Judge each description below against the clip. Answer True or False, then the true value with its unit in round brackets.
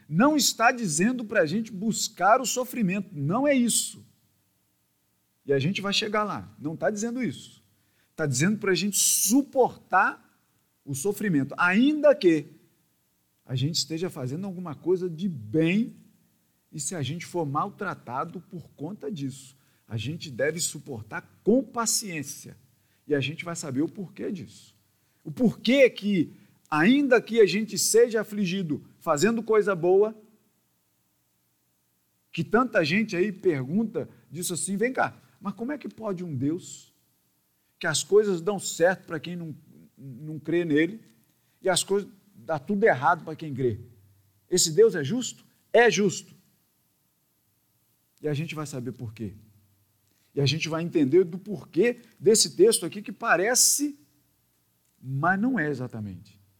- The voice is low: False (170 Hz)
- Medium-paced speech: True (150 wpm)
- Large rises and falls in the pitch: True (7.8 semitones)